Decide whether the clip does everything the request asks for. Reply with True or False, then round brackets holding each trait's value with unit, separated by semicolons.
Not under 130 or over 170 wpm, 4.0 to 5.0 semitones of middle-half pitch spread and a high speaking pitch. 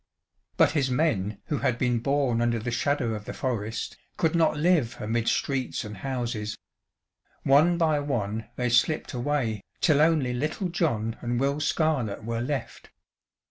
False (155 wpm; 4.5 semitones; 125 Hz)